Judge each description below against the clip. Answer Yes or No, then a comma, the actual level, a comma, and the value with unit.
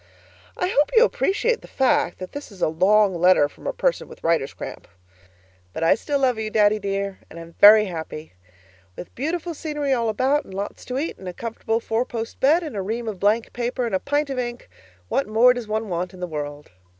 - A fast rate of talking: Yes, fast, 220 wpm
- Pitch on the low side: No, high, 225 Hz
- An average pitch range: No, wide, 6.4 semitones